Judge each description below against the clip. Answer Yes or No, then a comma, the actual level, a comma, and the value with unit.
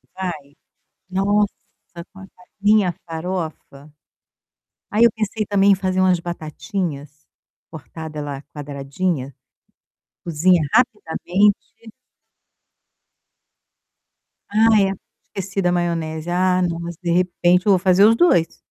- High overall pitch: No, medium, 180 Hz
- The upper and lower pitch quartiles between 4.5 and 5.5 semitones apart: No, average, 3.6 semitones